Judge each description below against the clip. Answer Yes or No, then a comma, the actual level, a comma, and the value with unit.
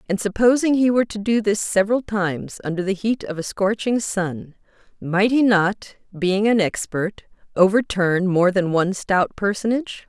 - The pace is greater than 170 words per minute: No, average, 165 wpm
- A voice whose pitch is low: No, high, 200 Hz